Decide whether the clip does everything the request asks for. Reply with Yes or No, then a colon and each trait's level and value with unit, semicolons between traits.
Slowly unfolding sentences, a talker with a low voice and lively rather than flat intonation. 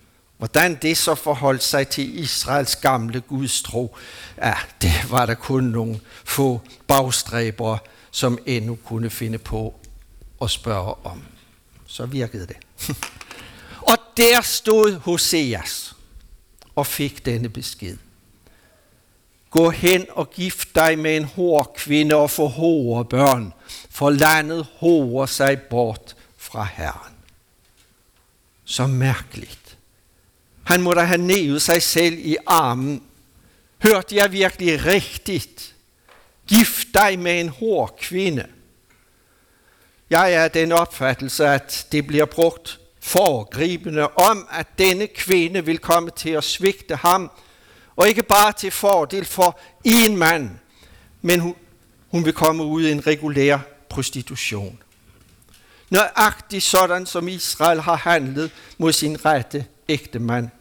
No: slow, 125 wpm; medium, 150 Hz; wide, 6.3 semitones